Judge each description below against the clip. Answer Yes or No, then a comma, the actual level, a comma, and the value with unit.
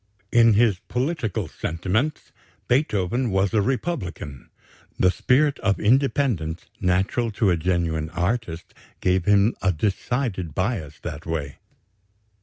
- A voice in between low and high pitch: No, low, 100 Hz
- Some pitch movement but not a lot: No, wide, 5.8 semitones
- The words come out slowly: Yes, slow, 115 wpm